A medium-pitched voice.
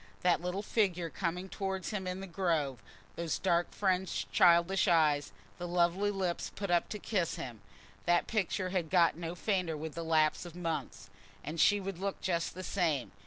Yes: medium, 175 Hz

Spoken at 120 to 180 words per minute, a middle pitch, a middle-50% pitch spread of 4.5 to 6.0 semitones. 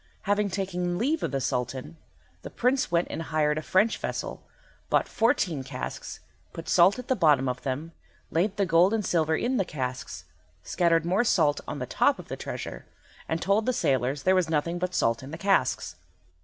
No: average, 195 wpm; medium, 170 Hz; average, 4.9 semitones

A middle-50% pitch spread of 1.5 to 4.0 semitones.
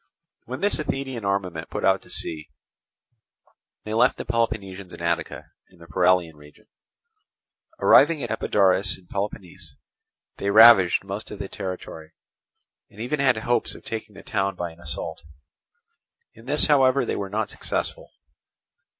No: average, 4.4 semitones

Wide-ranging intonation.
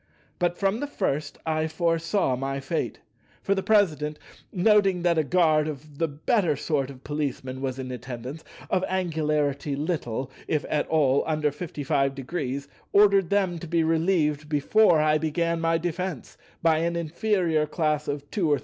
No: average, 3.4 semitones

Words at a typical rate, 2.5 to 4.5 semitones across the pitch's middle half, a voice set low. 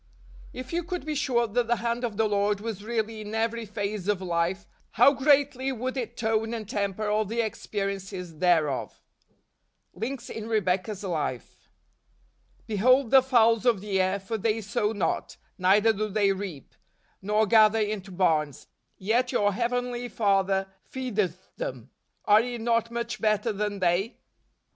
No: average, 160 wpm; average, 3.1 semitones; high, 215 Hz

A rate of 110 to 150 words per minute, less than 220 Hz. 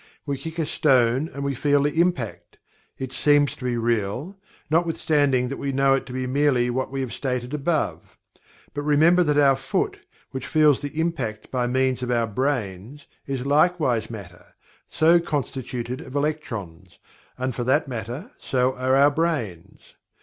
No: average, 165 wpm; low, 135 Hz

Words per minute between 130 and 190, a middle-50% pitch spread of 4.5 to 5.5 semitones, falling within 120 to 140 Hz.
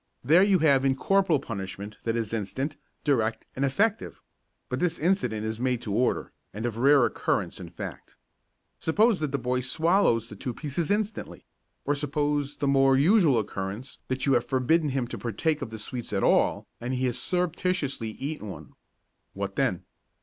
Yes: average, 175 wpm; average, 5.2 semitones; low, 135 Hz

